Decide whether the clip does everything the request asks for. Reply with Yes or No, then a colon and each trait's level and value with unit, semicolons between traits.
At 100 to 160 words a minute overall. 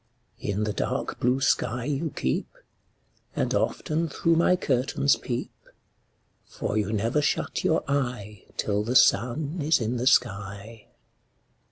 Yes: slow, 135 wpm